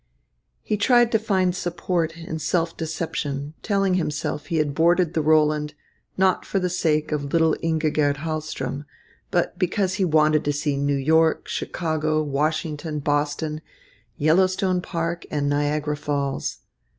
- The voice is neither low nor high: Yes, medium, 155 Hz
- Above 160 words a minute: No, average, 140 wpm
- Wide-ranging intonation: No, average, 2.7 semitones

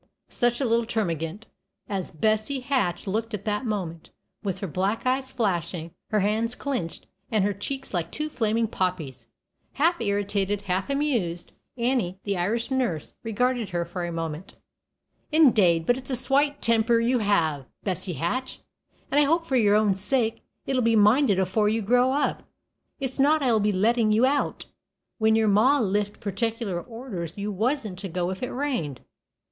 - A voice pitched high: Yes, high, 215 Hz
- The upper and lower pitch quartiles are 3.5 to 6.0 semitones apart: Yes, average, 4.9 semitones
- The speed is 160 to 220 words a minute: Yes, average, 170 wpm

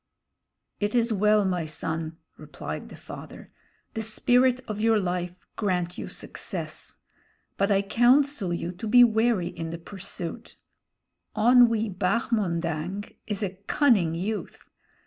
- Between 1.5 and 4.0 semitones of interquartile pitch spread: No, average, 4.4 semitones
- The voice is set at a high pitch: Yes, high, 205 Hz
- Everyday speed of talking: No, slow, 125 wpm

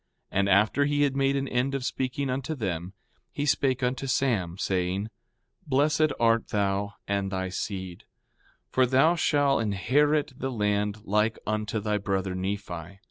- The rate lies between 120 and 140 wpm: No, average, 155 wpm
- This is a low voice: Yes, low, 110 Hz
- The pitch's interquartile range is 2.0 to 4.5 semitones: No, wide, 5.6 semitones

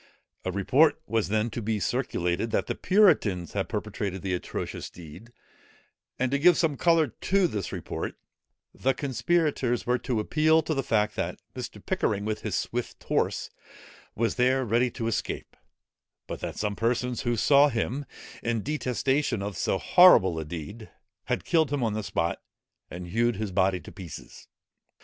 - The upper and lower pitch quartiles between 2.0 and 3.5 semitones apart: No, wide, 5.5 semitones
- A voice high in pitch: No, low, 115 Hz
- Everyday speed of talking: Yes, average, 165 wpm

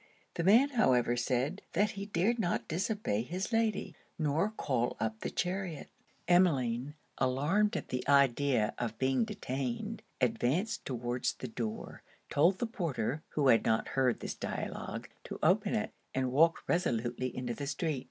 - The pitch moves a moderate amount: No, wide, 7.1 semitones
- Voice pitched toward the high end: No, medium, 140 Hz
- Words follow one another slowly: No, average, 150 wpm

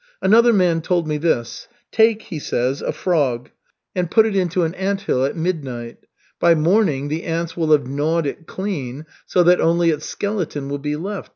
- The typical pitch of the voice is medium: Yes, medium, 165 Hz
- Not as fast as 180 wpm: No, average, 185 wpm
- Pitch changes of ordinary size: Yes, average, 4.2 semitones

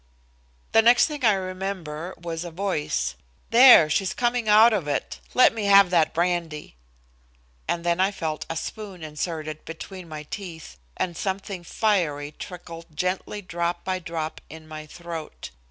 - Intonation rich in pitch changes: No, average, 3.8 semitones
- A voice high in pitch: No, medium, 175 Hz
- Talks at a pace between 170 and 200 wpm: No, average, 155 wpm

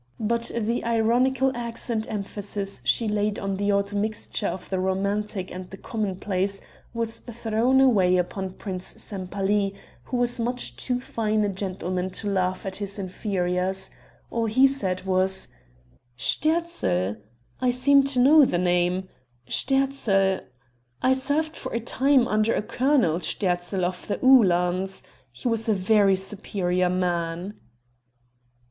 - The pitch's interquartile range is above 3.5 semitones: Yes, average, 4.1 semitones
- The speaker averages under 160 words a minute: Yes, slow, 135 wpm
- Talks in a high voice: Yes, high, 205 Hz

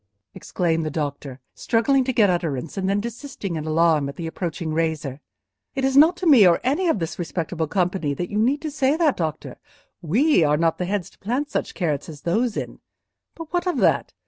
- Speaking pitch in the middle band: Yes, medium, 180 Hz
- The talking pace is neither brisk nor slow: No, fast, 210 wpm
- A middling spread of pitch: No, wide, 8.5 semitones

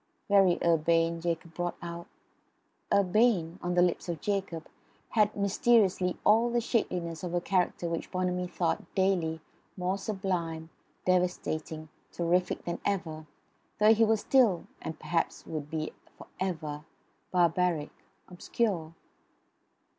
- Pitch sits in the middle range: Yes, medium, 180 Hz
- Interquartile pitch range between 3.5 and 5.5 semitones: No, average, 2.8 semitones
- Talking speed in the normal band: No, slow, 125 wpm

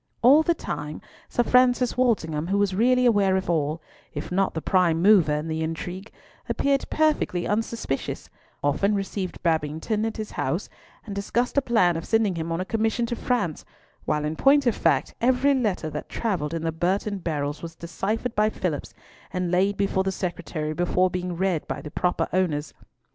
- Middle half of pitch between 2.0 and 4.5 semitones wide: No, wide, 5.5 semitones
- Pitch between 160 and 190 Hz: Yes, medium, 185 Hz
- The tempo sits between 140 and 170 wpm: No, average, 180 wpm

